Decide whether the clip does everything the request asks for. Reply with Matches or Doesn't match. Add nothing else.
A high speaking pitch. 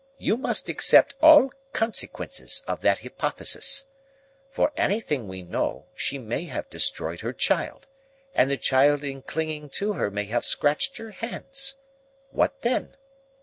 Doesn't match